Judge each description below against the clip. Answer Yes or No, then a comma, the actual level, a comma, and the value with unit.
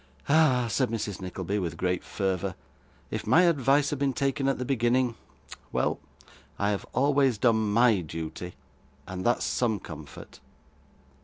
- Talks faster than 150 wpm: No, average, 145 wpm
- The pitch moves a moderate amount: No, wide, 6.4 semitones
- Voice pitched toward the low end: Yes, low, 115 Hz